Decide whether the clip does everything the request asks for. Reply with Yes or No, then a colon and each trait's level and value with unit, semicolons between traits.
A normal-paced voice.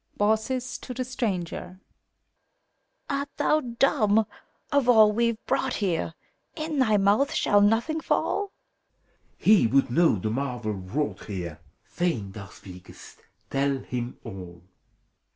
No: slow, 125 wpm